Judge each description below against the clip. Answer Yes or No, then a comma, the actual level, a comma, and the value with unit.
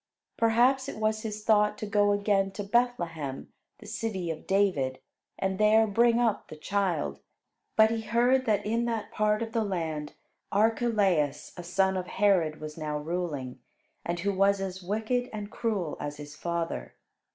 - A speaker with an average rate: Yes, average, 165 wpm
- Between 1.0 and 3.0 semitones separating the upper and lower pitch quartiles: No, average, 4.4 semitones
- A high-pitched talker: Yes, high, 200 Hz